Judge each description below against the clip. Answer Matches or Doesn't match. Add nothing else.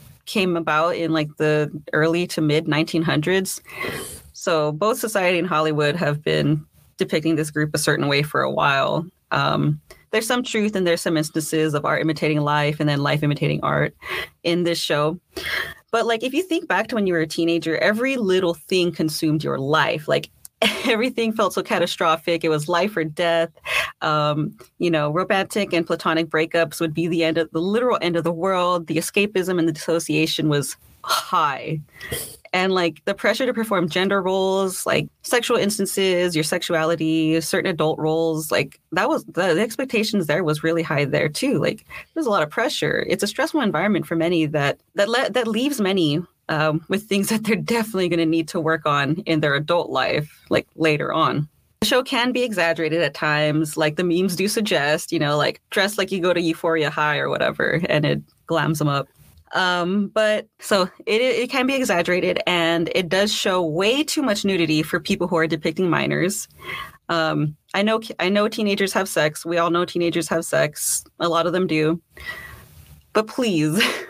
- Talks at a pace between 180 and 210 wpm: Matches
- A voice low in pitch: Doesn't match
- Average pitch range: Matches